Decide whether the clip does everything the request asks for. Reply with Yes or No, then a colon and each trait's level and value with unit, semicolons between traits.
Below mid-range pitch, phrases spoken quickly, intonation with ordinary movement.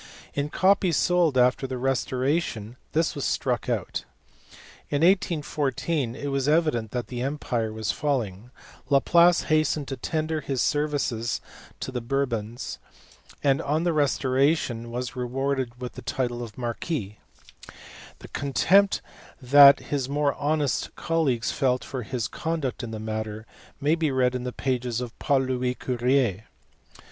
No: low, 130 Hz; average, 140 wpm; average, 3.5 semitones